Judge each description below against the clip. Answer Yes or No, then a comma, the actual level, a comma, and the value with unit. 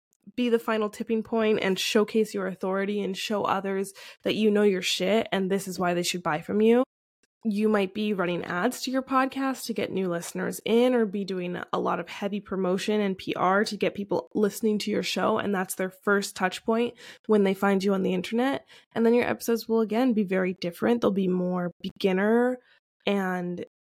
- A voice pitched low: No, high, 205 Hz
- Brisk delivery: Yes, fast, 210 wpm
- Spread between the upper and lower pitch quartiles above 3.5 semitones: No, average, 3.2 semitones